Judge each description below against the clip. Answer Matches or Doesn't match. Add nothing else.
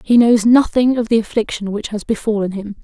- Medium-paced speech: Doesn't match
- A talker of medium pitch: Doesn't match